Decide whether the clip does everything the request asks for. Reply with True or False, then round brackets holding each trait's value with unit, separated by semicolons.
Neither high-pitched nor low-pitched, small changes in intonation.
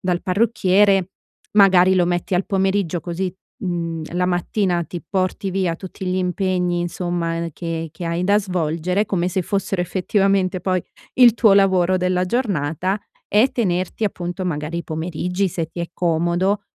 True (180 Hz; 2.0 semitones)